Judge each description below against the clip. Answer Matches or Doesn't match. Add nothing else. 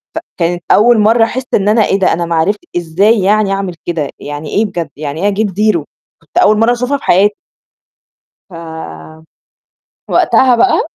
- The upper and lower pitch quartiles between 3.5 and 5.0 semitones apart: Matches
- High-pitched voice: Matches